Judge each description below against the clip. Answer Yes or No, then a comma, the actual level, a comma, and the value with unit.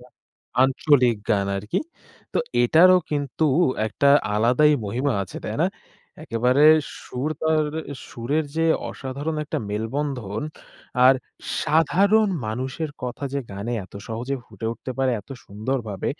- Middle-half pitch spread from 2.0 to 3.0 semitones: No, average, 4.8 semitones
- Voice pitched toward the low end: Yes, low, 130 Hz